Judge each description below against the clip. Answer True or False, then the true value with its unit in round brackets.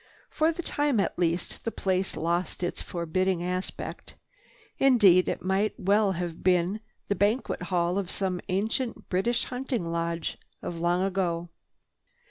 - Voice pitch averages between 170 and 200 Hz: True (185 Hz)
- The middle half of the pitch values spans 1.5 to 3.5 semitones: True (3.0 semitones)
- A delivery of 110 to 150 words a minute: True (140 wpm)